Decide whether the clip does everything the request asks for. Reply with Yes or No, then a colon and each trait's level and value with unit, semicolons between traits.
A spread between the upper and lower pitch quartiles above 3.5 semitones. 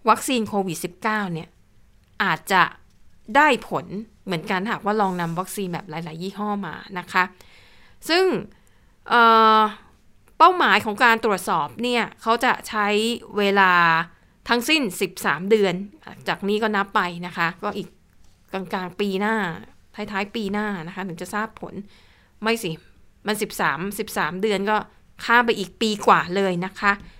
No: average, 3.1 semitones